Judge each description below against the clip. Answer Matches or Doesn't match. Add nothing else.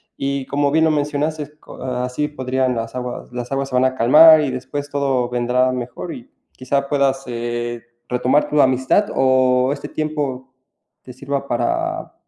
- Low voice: Matches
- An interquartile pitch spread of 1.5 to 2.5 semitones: Matches